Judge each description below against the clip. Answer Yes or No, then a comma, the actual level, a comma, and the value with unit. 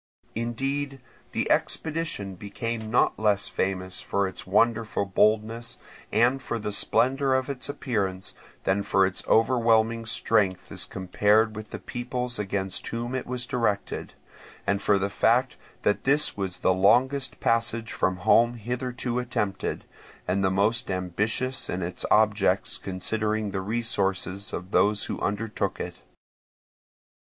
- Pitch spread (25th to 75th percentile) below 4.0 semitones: Yes, average, 3.6 semitones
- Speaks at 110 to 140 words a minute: Yes, slow, 135 wpm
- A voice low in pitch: Yes, low, 110 Hz